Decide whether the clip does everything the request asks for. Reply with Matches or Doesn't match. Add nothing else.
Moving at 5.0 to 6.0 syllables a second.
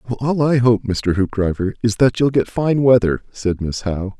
Matches